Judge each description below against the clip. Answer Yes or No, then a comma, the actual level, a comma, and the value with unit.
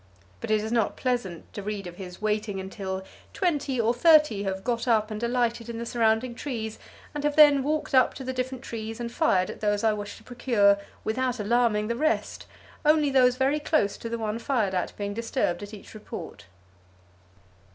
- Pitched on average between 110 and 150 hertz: No, high, 230 Hz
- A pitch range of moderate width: Yes, average, 3.6 semitones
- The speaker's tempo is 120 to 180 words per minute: No, average, 195 wpm